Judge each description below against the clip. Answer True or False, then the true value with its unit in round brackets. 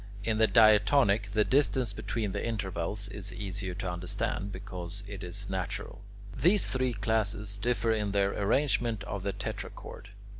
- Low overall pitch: True (100 Hz)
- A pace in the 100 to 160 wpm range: True (150 wpm)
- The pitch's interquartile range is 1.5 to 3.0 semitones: True (2.4 semitones)